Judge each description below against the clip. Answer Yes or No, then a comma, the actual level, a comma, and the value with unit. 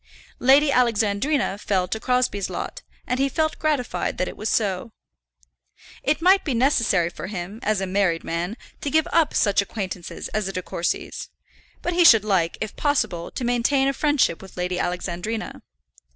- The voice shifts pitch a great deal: Yes, wide, 6.6 semitones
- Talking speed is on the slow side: No, average, 170 wpm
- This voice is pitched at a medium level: No, high, 215 Hz